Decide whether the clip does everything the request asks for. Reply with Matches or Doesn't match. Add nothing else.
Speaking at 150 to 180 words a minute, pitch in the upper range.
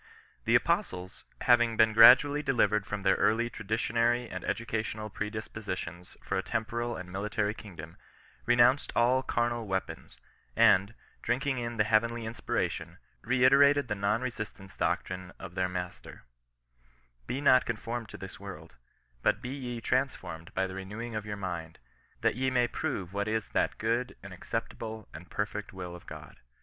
Doesn't match